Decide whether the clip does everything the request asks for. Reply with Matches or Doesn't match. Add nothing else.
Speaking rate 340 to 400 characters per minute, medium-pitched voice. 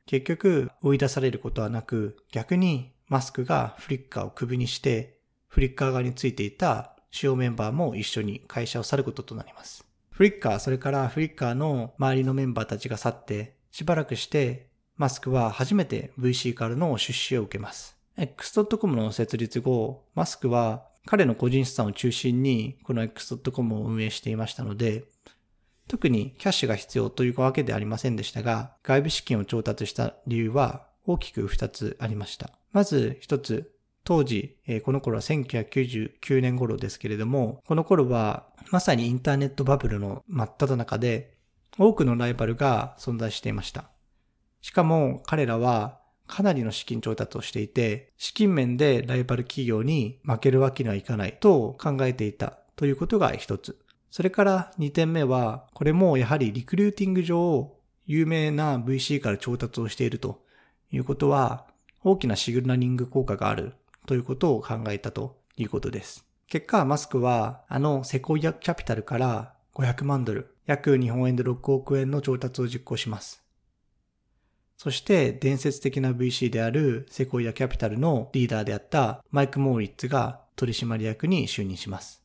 Doesn't match